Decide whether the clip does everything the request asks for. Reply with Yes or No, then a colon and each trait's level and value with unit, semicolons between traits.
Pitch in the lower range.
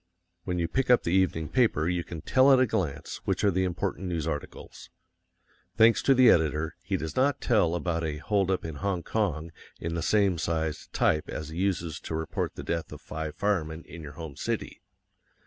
Yes: very low, 85 Hz